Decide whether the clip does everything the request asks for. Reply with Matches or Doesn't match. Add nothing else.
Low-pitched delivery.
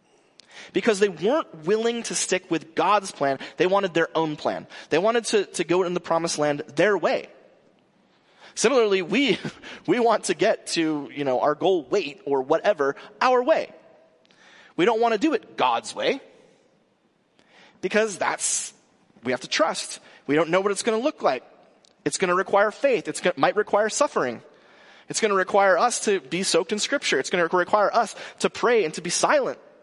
Doesn't match